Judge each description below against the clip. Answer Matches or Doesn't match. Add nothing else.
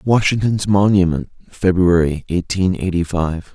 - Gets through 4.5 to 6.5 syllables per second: Doesn't match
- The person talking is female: Doesn't match